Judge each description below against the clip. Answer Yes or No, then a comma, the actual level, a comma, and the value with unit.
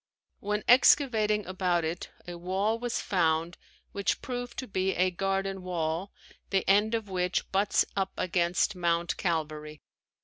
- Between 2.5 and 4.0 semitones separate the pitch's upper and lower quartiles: Yes, average, 3.2 semitones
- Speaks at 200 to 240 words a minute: No, average, 140 wpm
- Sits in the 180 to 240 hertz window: Yes, high, 190 Hz